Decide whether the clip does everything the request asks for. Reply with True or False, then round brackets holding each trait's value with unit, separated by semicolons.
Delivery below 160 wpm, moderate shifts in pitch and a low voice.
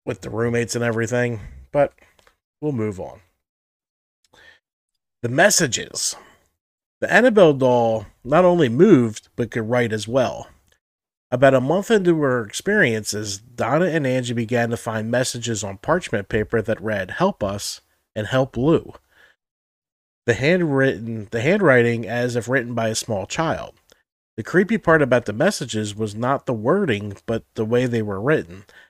True (150 wpm; 3.7 semitones; 120 Hz)